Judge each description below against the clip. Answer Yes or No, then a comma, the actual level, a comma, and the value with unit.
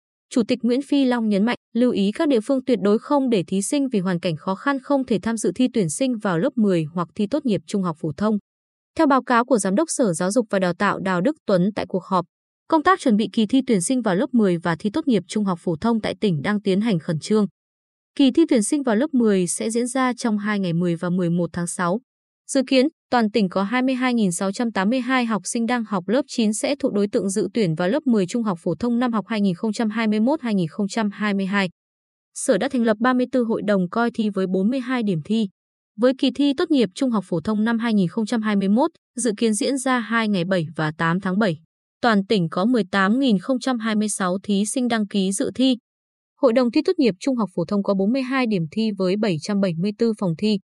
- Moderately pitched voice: No, high, 220 Hz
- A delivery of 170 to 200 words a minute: No, average, 230 wpm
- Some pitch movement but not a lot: Yes, average, 4.6 semitones